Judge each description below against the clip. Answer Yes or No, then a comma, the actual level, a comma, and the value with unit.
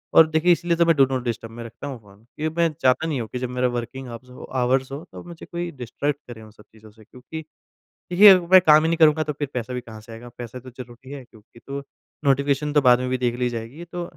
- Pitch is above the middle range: No, low, 130 Hz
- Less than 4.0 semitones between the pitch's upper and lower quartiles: No, average, 4.4 semitones